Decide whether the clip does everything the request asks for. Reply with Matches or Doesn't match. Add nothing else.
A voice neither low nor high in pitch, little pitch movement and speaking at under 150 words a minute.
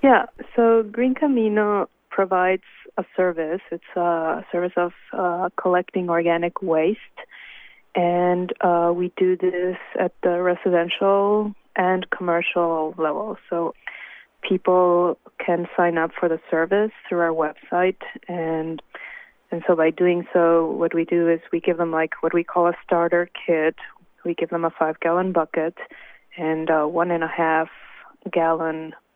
Matches